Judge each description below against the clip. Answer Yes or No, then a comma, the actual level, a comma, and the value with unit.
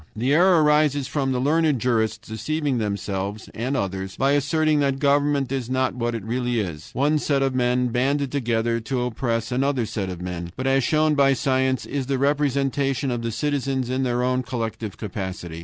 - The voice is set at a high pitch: No, low, 130 Hz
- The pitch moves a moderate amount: Yes, average, 3.6 semitones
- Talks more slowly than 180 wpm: No, average, 185 wpm